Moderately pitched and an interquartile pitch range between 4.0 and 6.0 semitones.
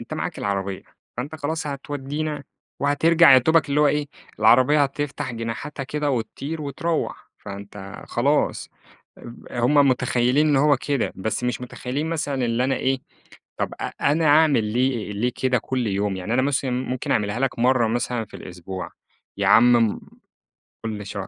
No: low, 130 Hz; average, 4.3 semitones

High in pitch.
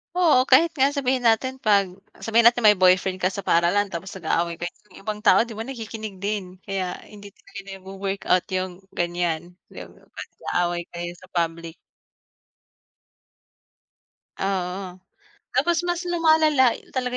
Yes: high, 195 Hz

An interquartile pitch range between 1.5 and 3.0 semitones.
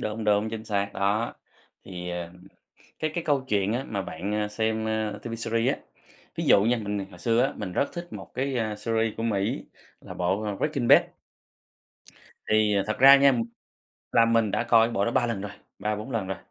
Yes: narrow, 2.4 semitones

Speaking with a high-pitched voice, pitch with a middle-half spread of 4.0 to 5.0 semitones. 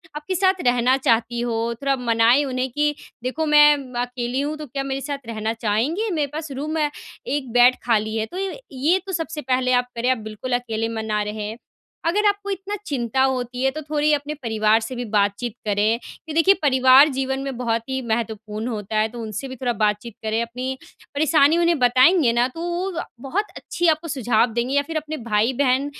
Yes: very high, 255 Hz; average, 4.7 semitones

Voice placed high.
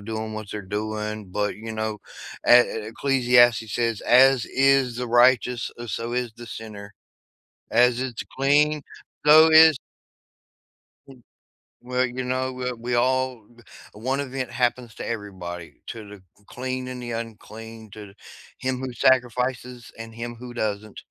No: low, 120 Hz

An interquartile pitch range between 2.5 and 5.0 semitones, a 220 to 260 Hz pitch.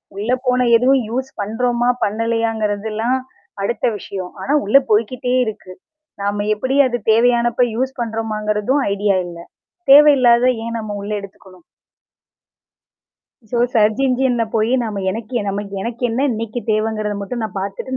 Yes: average, 3.0 semitones; high, 225 Hz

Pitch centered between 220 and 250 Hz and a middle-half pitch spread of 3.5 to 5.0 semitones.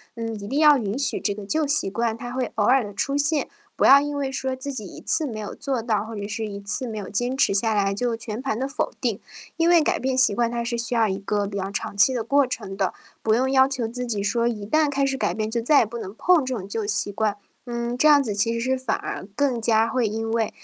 Yes: high, 235 Hz; average, 3.9 semitones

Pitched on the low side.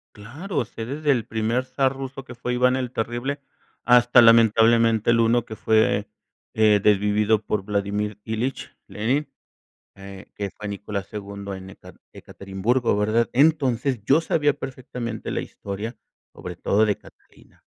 Yes: low, 115 Hz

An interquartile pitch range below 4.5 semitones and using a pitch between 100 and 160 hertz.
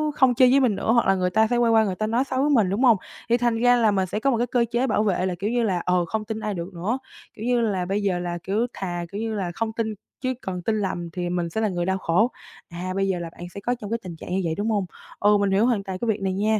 No: average, 3.9 semitones; high, 210 Hz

